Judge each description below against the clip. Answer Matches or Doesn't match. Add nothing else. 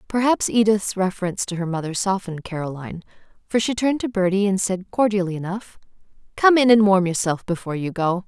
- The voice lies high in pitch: Matches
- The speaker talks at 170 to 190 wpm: Matches